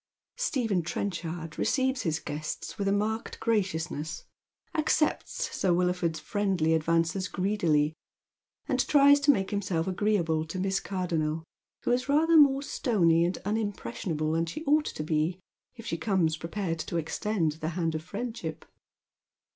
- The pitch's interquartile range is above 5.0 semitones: Yes, wide, 5.4 semitones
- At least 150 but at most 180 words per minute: No, average, 140 wpm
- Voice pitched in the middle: Yes, medium, 180 Hz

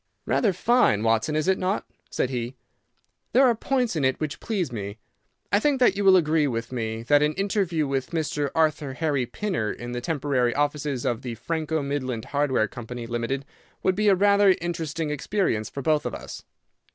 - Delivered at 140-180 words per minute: No, average, 190 wpm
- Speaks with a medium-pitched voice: Yes, medium, 150 Hz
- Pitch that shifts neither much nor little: No, wide, 6.8 semitones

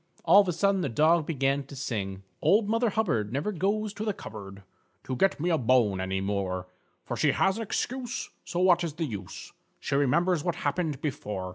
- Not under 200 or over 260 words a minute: Yes, fast, 205 wpm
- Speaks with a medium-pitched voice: Yes, medium, 150 Hz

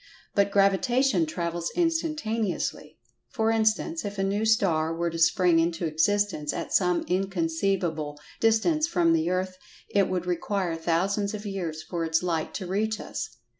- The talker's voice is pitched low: No, medium, 185 Hz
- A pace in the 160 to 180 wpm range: No, average, 150 wpm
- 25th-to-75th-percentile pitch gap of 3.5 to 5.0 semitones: Yes, average, 4.0 semitones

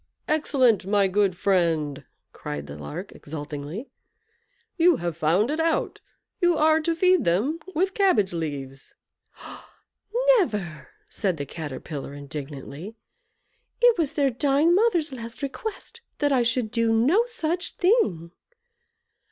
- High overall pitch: Yes, high, 225 Hz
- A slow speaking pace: Yes, slow, 125 wpm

